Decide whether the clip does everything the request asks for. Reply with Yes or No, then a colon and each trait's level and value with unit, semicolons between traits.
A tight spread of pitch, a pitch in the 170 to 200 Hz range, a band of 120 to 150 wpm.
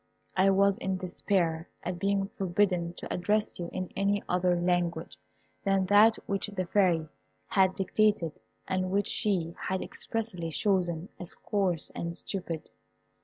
Yes: narrow, 2.3 semitones; medium, 185 Hz; average, 140 wpm